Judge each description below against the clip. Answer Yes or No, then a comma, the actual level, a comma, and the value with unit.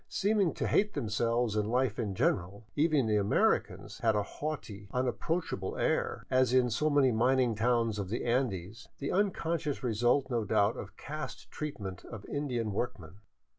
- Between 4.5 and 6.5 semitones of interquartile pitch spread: Yes, average, 5.1 semitones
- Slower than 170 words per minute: Yes, average, 160 wpm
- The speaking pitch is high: No, low, 120 Hz